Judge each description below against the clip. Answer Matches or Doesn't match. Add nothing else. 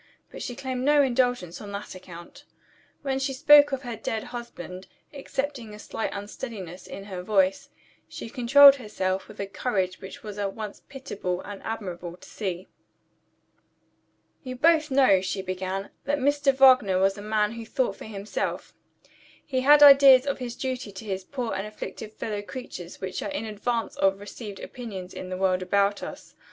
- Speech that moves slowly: Doesn't match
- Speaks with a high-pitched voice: Matches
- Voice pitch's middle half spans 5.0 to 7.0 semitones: Matches